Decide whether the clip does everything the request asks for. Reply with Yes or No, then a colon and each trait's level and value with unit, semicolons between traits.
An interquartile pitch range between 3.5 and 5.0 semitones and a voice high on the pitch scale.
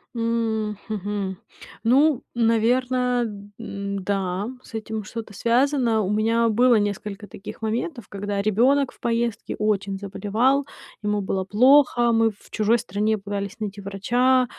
No: average, 2.8 semitones; high, 220 Hz